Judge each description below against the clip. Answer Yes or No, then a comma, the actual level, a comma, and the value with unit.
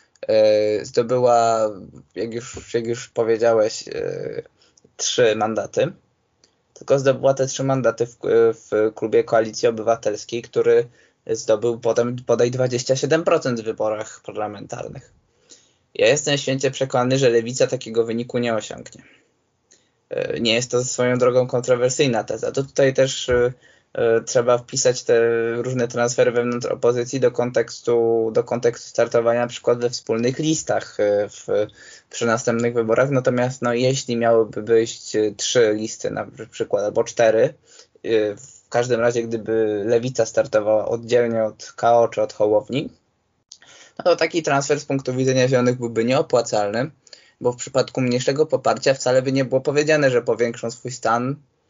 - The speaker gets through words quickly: No, average, 130 wpm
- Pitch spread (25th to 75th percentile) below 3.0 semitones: No, average, 3.3 semitones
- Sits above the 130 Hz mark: No, low, 125 Hz